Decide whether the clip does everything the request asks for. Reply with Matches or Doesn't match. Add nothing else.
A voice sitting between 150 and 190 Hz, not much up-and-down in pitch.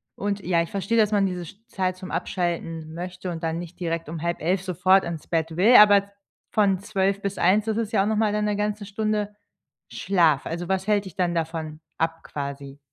Doesn't match